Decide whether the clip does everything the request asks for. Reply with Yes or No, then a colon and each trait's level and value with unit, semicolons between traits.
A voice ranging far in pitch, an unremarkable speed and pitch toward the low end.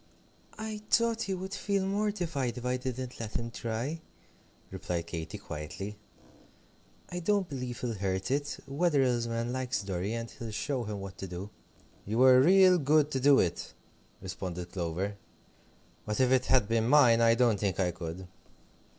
Yes: wide, 6.4 semitones; average, 165 wpm; low, 120 Hz